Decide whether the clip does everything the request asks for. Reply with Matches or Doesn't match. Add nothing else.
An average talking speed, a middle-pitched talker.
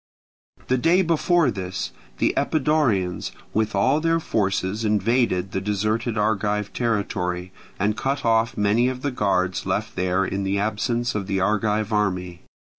Doesn't match